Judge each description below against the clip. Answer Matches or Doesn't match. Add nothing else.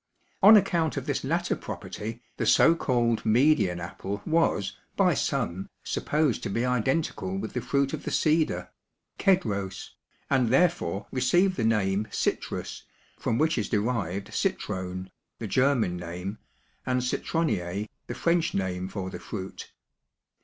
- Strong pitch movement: Matches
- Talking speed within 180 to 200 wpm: Doesn't match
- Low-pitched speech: Matches